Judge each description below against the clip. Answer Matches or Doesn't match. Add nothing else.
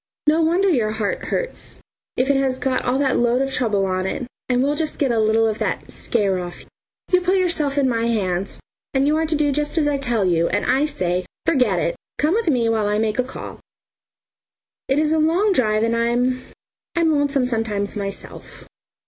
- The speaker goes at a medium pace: Doesn't match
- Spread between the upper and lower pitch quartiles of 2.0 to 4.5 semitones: Doesn't match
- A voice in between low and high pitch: Doesn't match